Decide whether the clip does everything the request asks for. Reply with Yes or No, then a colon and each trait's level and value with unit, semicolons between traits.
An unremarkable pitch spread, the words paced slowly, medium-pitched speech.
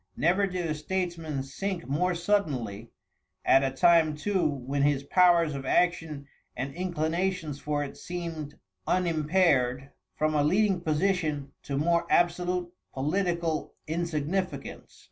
Yes: average, 3.7 semitones; slow, 125 wpm; medium, 160 Hz